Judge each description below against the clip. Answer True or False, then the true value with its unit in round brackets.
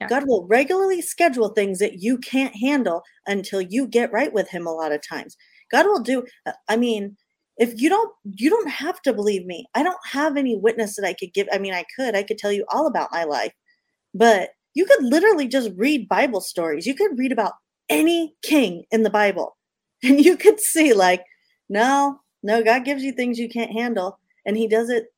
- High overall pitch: True (235 Hz)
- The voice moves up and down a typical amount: False (5.9 semitones)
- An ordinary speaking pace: False (210 wpm)